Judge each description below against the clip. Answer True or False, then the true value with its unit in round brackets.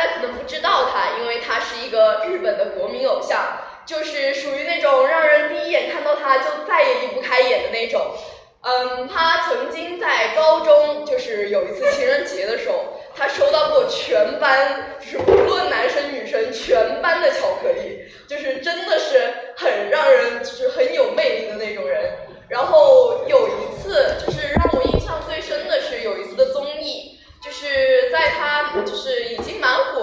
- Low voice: False (325 Hz)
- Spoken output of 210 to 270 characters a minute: True (260 characters per minute)